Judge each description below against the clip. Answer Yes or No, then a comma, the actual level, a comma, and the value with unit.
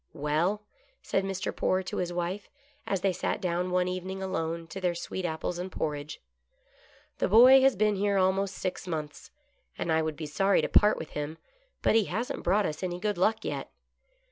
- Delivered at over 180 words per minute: Yes, average, 200 wpm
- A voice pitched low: No, medium, 185 Hz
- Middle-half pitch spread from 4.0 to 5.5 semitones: No, average, 2.9 semitones